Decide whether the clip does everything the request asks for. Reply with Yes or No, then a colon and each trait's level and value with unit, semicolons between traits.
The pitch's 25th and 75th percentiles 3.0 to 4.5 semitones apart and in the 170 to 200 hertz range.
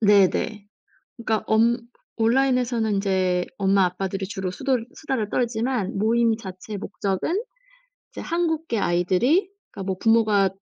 No: average, 3.7 semitones; high, 220 Hz